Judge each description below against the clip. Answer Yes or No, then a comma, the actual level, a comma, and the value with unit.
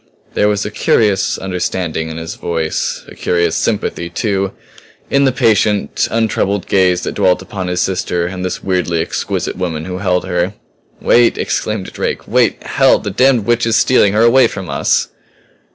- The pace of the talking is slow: No, average, 170 wpm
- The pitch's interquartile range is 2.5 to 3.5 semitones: Yes, average, 3.2 semitones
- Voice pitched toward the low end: Yes, very low, 95 Hz